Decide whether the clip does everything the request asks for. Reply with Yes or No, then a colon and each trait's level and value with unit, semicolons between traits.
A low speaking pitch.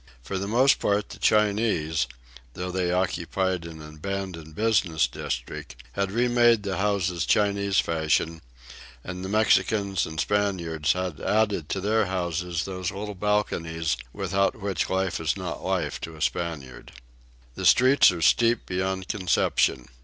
Yes: very low, 95 Hz